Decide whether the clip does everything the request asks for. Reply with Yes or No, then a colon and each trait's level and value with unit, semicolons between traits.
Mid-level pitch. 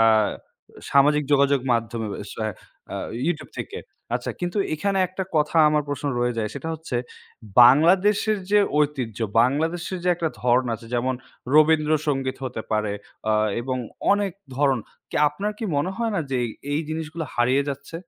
Yes: medium, 150 Hz